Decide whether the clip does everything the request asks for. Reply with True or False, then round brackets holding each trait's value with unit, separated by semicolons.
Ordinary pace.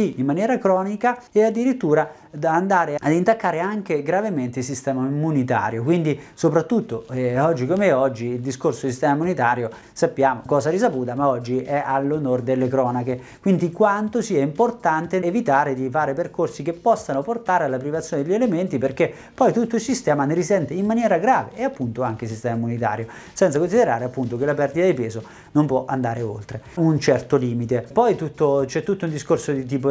False (175 wpm)